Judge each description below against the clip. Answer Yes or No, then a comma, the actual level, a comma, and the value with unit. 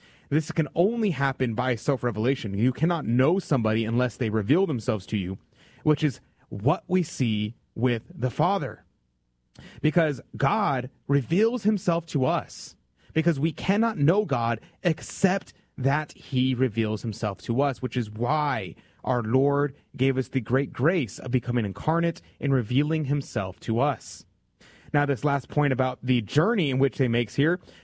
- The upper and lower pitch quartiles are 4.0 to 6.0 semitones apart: Yes, average, 4.6 semitones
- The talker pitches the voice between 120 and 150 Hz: Yes, low, 135 Hz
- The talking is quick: No, average, 155 wpm